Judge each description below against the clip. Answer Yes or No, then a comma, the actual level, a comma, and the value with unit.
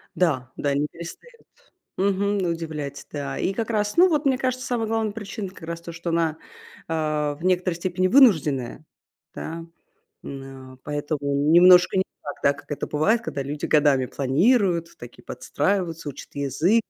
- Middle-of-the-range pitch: Yes, medium, 165 Hz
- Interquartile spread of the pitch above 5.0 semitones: Yes, wide, 5.6 semitones